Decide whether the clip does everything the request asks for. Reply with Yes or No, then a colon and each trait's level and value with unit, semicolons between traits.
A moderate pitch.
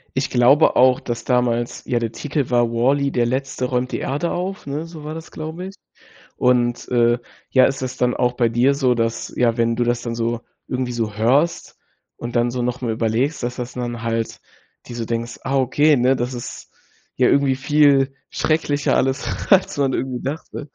No: low, 125 Hz